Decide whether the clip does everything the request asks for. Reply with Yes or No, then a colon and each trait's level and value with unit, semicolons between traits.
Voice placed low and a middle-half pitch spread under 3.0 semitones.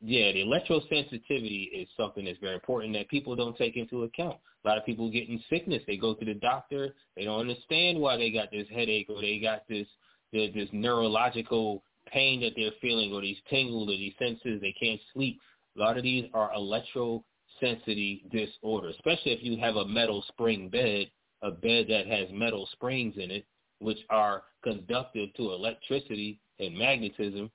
Yes: low, 110 Hz; narrow, 2.5 semitones